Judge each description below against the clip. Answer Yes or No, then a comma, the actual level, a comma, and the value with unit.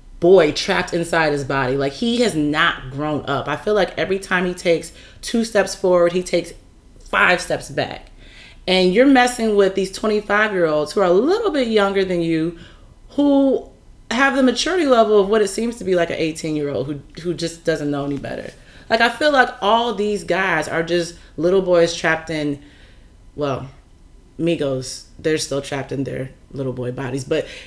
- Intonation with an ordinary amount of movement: No, wide, 6.4 semitones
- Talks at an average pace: Yes, average, 195 wpm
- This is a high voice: No, medium, 170 Hz